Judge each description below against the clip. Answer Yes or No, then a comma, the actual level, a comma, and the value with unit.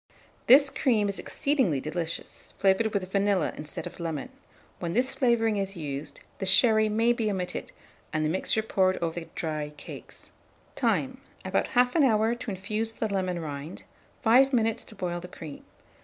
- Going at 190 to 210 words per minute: No, average, 165 wpm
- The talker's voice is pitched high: Yes, high, 195 Hz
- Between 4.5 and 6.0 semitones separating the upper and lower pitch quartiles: Yes, average, 5.0 semitones